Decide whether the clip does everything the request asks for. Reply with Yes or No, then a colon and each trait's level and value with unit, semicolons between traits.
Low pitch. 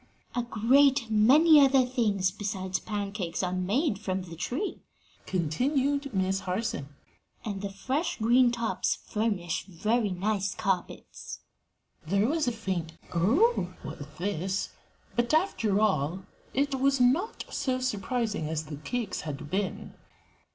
No: high, 210 Hz